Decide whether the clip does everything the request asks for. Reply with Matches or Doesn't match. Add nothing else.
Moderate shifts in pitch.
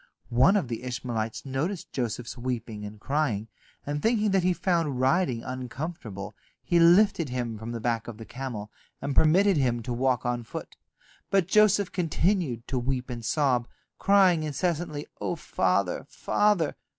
Doesn't match